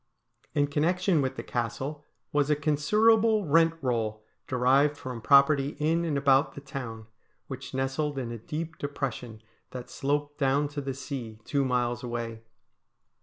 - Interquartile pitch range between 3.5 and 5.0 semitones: No, average, 3.0 semitones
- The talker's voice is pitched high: No, medium, 140 Hz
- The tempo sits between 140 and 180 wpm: Yes, average, 150 wpm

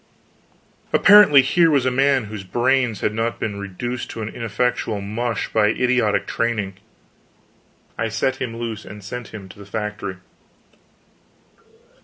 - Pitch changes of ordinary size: Yes, average, 3.2 semitones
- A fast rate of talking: No, average, 140 wpm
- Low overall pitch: Yes, low, 115 Hz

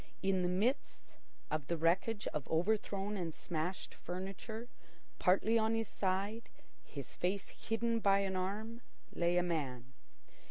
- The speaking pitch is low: No, high, 190 Hz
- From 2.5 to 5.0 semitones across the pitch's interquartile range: Yes, average, 4.0 semitones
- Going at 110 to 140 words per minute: Yes, slow, 135 wpm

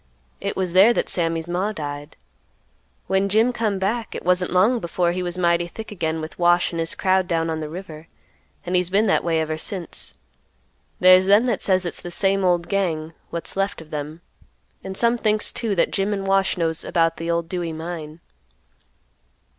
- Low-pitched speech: No, medium, 180 Hz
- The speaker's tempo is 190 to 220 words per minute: Yes, average, 195 wpm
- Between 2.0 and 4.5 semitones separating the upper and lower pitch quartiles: Yes, average, 2.9 semitones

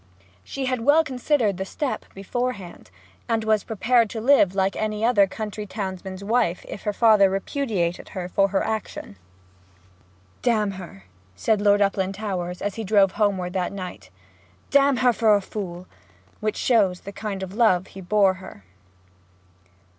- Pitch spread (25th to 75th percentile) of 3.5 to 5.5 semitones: No, average, 2.8 semitones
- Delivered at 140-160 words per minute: Yes, average, 155 wpm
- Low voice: No, high, 205 Hz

